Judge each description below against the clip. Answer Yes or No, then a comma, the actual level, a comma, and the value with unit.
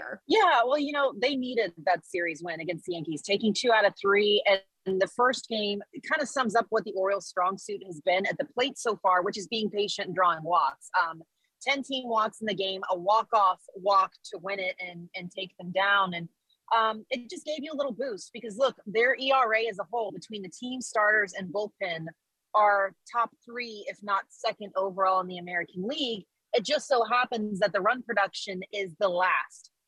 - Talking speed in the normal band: No, fast, 215 wpm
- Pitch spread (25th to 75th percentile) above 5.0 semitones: No, average, 4.0 semitones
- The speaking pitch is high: Yes, high, 205 Hz